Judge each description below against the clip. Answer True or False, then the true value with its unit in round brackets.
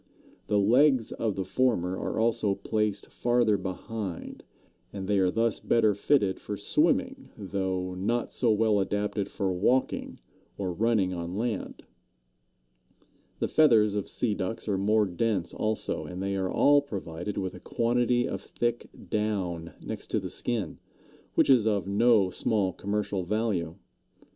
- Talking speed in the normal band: True (150 wpm)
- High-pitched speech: False (105 Hz)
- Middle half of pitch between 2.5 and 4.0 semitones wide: True (3.4 semitones)